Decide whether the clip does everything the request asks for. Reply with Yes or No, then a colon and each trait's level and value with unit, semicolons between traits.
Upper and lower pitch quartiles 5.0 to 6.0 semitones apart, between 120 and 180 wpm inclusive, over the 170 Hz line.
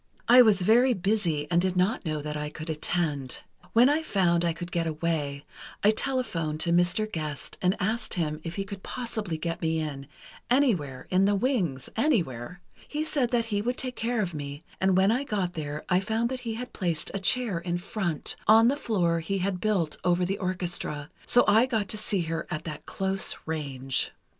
No: wide, 5.5 semitones; average, 195 wpm; medium, 185 Hz